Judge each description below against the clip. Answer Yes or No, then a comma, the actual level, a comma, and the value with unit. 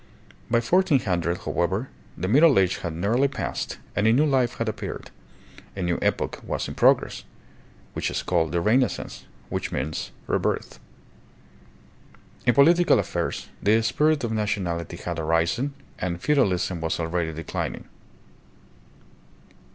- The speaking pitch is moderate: No, low, 100 Hz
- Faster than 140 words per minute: No, slow, 135 wpm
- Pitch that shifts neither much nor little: No, wide, 6.9 semitones